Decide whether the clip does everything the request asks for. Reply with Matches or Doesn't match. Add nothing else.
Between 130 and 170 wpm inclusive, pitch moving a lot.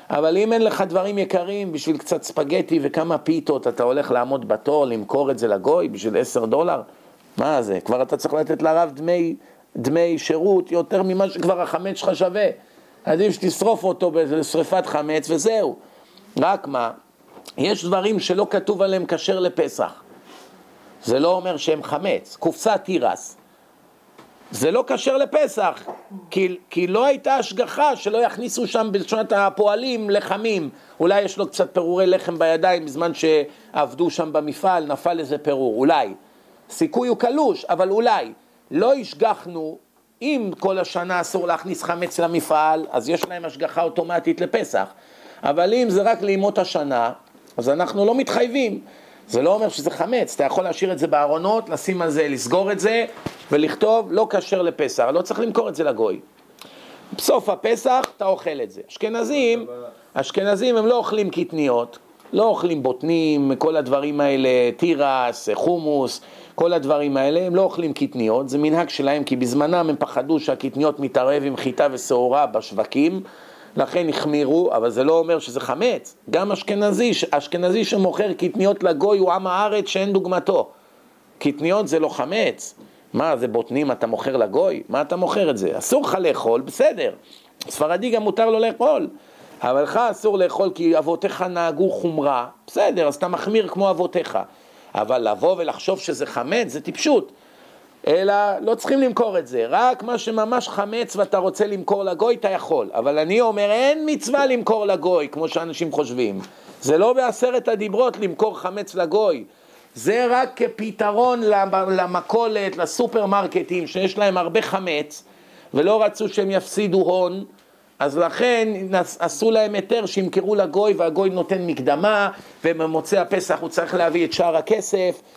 Doesn't match